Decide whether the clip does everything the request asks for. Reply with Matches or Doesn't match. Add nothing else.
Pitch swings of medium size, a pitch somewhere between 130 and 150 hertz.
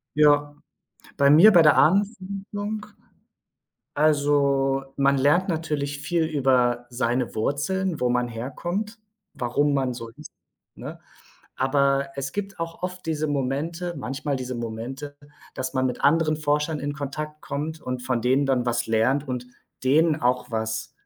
Matches